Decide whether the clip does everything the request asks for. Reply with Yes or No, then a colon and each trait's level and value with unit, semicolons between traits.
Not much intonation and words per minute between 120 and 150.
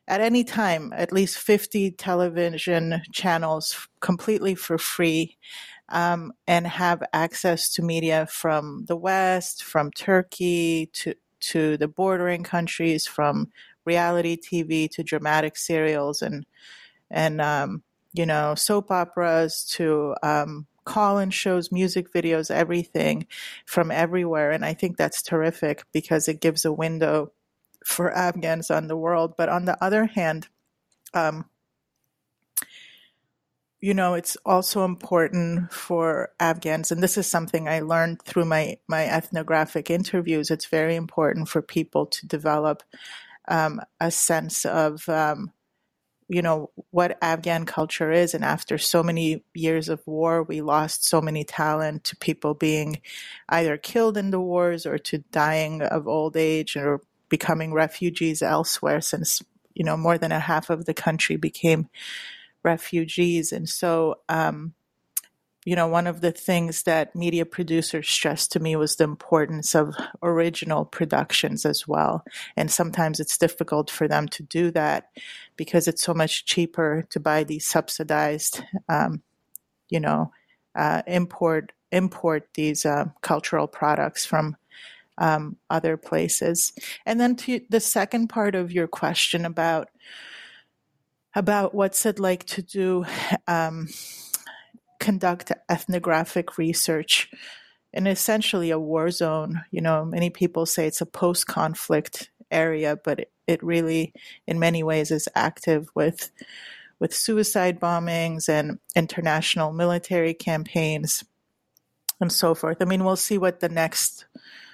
Yes: narrow, 2.1 semitones; average, 140 wpm